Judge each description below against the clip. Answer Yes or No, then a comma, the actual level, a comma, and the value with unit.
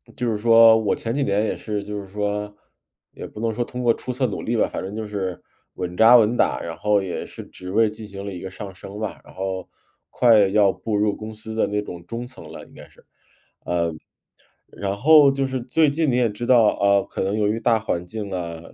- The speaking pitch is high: No, low, 105 Hz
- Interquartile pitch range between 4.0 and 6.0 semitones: No, average, 2.7 semitones